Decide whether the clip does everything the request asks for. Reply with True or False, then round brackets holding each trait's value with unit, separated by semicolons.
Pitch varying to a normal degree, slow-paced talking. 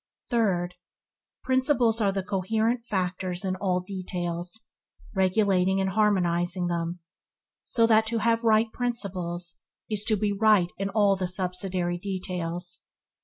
True (3.4 semitones; 125 wpm)